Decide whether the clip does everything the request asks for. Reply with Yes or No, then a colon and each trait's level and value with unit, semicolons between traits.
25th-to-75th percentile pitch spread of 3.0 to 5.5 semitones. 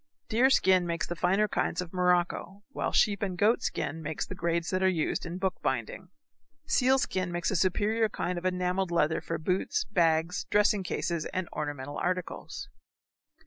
No: narrow, 2.4 semitones